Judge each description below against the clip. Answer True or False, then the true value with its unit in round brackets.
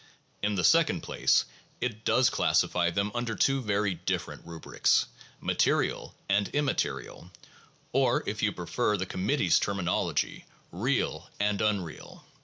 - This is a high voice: False (105 Hz)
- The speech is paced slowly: True (130 wpm)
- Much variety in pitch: False (4.2 semitones)